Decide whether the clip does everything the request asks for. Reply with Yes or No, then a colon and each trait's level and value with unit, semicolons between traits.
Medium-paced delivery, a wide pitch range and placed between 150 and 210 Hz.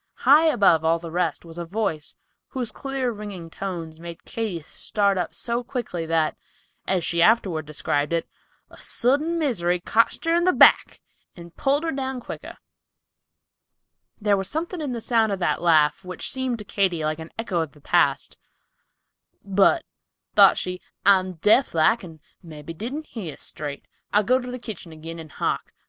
Yes: average, 175 wpm; wide, 6.6 semitones; high, 190 Hz